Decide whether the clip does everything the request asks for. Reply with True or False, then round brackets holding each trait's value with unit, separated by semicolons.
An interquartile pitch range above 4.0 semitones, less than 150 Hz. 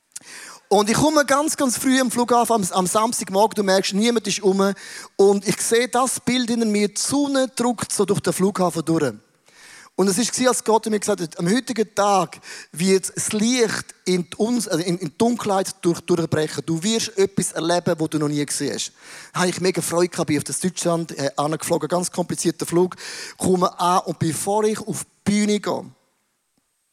False (4.4 semitones; 190 Hz)